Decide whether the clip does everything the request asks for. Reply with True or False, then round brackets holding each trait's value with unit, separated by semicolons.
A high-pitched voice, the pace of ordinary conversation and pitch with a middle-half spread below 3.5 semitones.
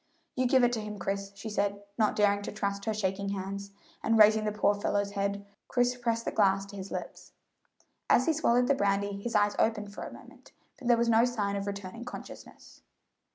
False (205 Hz; 210 wpm; 2.5 semitones)